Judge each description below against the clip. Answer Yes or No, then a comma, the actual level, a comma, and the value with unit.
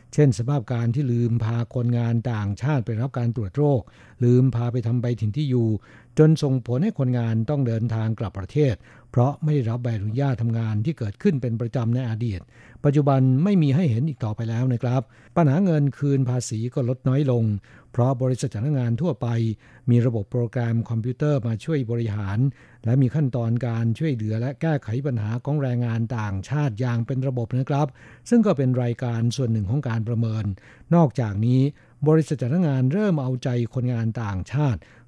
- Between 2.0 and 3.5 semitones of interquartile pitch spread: Yes, average, 3.1 semitones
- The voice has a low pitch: Yes, low, 125 Hz